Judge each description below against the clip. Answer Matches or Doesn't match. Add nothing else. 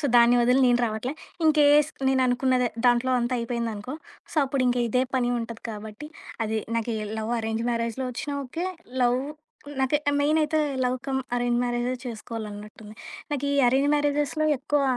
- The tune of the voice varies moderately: Matches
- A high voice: Matches